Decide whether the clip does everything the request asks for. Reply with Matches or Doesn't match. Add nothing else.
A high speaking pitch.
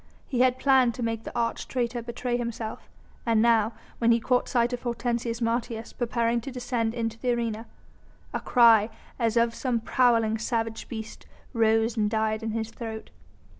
Matches